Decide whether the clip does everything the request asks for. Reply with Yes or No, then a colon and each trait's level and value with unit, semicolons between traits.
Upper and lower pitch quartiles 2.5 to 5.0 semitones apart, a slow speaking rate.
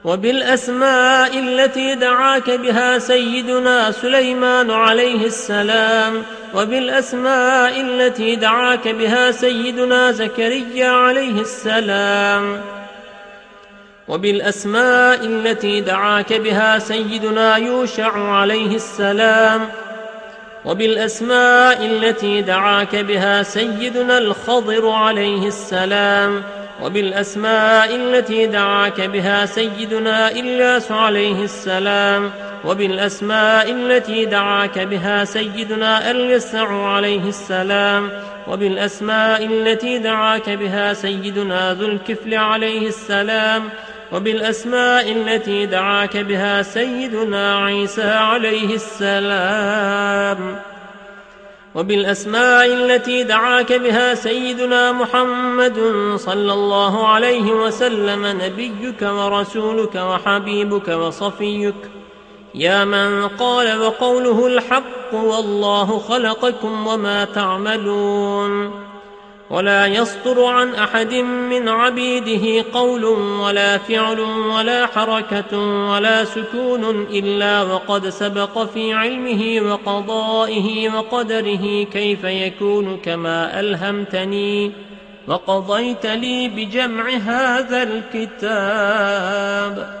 Yes: average, 2.8 semitones; slow, 80 wpm